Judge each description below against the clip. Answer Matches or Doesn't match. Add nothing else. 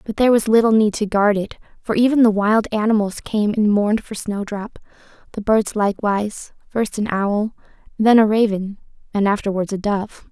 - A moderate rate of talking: Matches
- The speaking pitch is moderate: Doesn't match